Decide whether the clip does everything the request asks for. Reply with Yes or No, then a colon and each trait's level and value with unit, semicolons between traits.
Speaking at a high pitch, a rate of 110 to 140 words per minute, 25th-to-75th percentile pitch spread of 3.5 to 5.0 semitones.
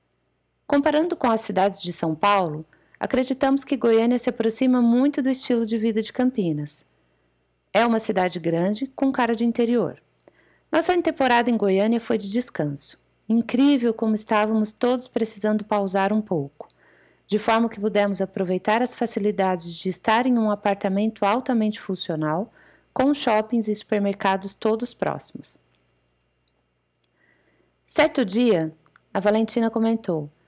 Yes: high, 215 Hz; average, 130 wpm; average, 4.0 semitones